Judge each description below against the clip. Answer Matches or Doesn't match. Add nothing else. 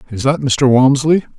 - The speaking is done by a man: Matches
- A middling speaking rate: Matches